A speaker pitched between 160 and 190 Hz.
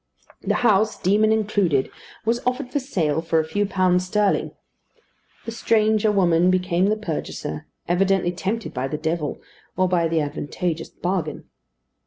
Yes: medium, 185 Hz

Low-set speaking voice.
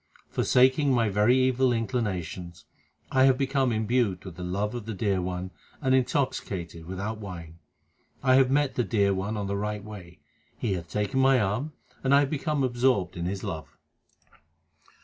Yes: low, 110 Hz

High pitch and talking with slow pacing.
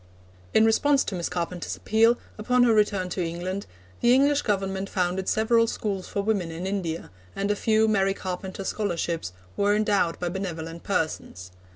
No: high, 195 Hz; average, 165 wpm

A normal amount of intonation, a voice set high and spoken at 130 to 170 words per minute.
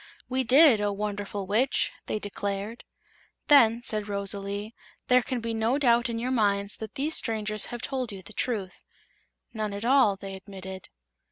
Yes: average, 3.2 semitones; high, 215 Hz; average, 165 wpm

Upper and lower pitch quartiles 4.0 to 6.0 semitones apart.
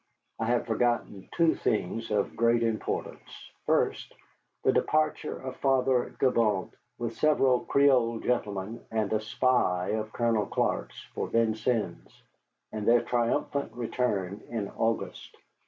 No: narrow, 2.5 semitones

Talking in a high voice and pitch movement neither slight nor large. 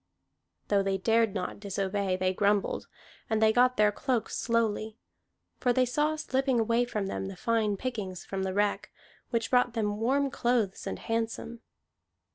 Yes: high, 220 Hz; average, 3.3 semitones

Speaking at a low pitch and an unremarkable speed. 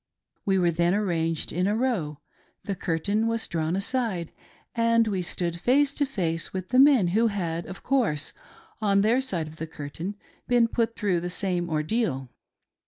No: high, 190 Hz; average, 170 wpm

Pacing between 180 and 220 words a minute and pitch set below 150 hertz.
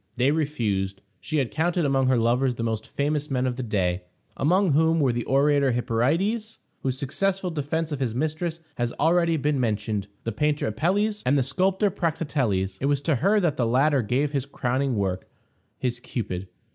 Yes: average, 185 wpm; medium, 140 Hz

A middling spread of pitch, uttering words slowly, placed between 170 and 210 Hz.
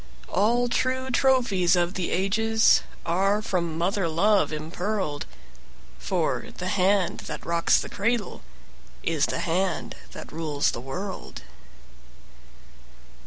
Yes: average, 4.0 semitones; slow, 115 wpm; medium, 185 Hz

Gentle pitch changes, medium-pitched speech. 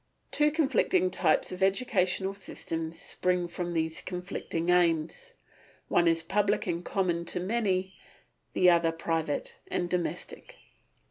No: average, 3.0 semitones; medium, 180 Hz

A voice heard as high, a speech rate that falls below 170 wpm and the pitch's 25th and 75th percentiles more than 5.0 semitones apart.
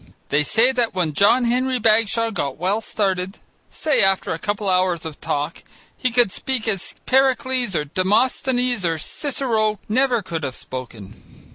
Yes: high, 210 Hz; average, 160 wpm; wide, 5.5 semitones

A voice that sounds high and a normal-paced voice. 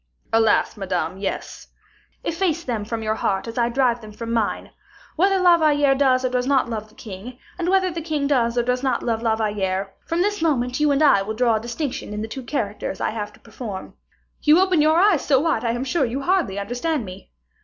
No: high, 245 Hz; fast, 230 wpm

